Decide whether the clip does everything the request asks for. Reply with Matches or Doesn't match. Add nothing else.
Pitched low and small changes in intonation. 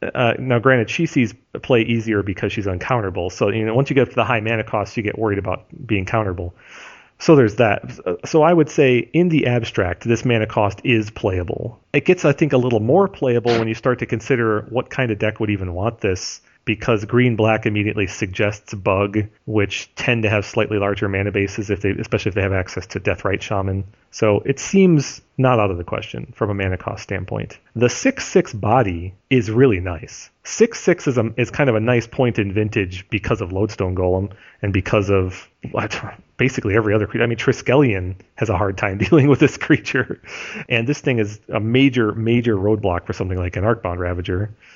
Doesn't match